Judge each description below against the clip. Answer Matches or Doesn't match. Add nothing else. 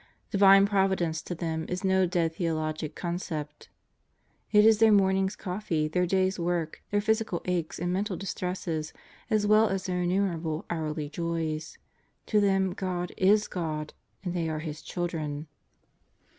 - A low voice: Doesn't match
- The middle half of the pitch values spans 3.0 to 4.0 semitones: Matches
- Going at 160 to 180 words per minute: Doesn't match